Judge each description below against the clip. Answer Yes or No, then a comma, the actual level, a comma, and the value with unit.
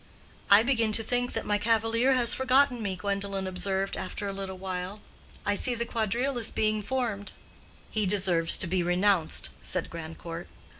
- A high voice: Yes, high, 205 Hz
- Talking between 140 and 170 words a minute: Yes, average, 165 wpm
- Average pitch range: Yes, average, 3.6 semitones